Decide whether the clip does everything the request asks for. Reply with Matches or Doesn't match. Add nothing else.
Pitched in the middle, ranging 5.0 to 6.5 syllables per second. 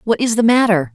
Doesn't match